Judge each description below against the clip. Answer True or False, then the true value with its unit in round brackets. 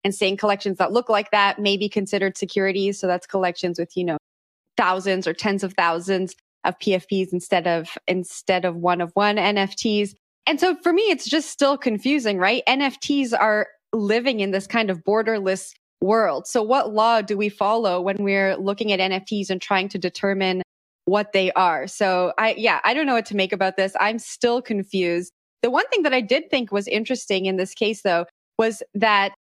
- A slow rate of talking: False (195 wpm)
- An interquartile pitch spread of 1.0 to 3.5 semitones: True (2.9 semitones)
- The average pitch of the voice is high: True (200 Hz)